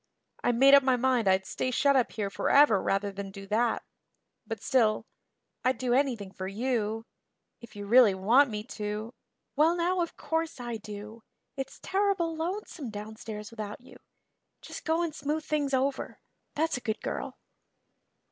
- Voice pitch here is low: No, high, 245 Hz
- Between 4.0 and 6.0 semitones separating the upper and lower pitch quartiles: Yes, average, 5.1 semitones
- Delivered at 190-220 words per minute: No, average, 165 wpm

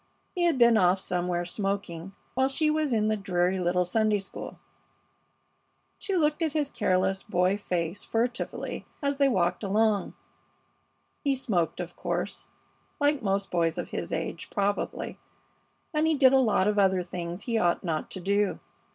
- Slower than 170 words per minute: Yes, average, 160 wpm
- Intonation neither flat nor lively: No, wide, 6.3 semitones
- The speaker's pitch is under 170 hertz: No, high, 200 Hz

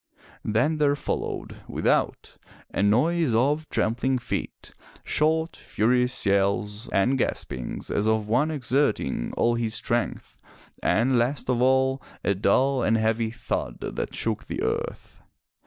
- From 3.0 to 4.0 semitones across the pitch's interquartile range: Yes, average, 3.6 semitones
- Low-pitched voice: Yes, low, 120 Hz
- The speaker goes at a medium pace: No, slow, 130 wpm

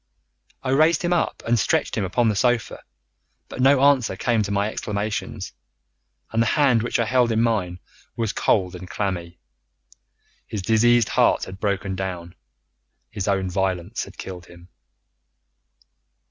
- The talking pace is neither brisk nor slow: Yes, average, 150 wpm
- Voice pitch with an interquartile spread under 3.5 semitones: No, average, 4.0 semitones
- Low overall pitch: Yes, low, 105 Hz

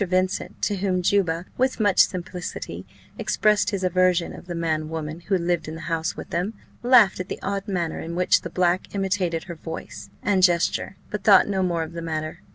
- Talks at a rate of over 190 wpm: Yes, average, 200 wpm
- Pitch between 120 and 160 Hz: No, medium, 180 Hz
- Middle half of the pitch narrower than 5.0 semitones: Yes, narrow, 2.5 semitones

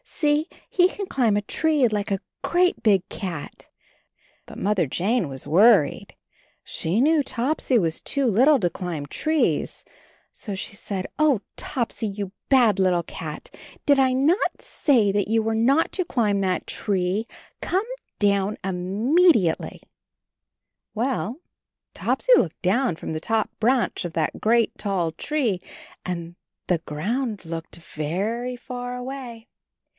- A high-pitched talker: Yes, high, 215 Hz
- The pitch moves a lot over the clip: Yes, wide, 6.1 semitones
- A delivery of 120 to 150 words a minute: Yes, average, 140 wpm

